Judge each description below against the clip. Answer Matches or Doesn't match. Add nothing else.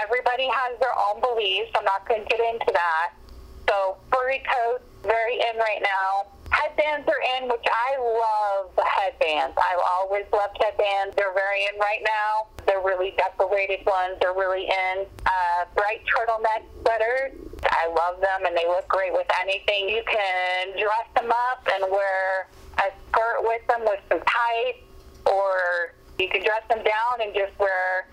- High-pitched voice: Matches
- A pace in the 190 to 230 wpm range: Doesn't match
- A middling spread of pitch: Matches